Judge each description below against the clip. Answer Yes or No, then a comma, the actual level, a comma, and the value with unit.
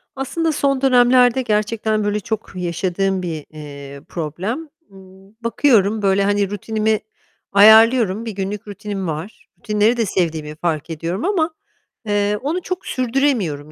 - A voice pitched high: Yes, high, 205 Hz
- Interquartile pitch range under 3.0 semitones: No, average, 4.3 semitones